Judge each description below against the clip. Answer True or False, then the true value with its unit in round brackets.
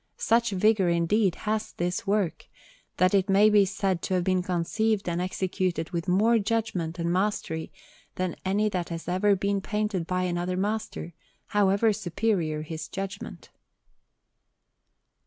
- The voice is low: False (190 Hz)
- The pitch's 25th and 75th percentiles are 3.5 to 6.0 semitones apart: False (3.1 semitones)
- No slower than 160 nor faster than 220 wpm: False (145 wpm)